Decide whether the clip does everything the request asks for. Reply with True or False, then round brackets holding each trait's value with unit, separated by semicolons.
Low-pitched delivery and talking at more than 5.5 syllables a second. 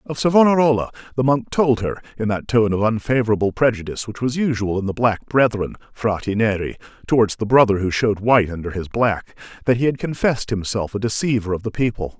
True (115 Hz; 6.0 syllables/s)